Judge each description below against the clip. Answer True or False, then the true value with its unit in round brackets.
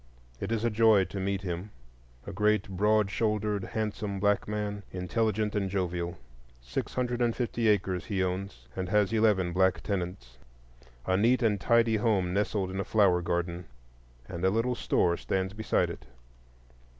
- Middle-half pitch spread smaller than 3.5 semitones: True (2.9 semitones)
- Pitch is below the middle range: True (100 Hz)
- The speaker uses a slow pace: False (160 wpm)